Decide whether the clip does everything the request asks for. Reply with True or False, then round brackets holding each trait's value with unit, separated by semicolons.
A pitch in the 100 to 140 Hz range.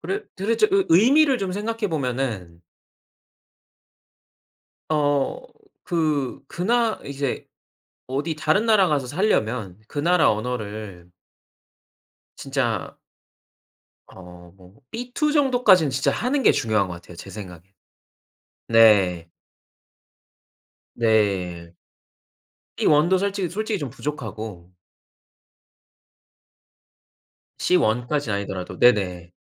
True (135 Hz)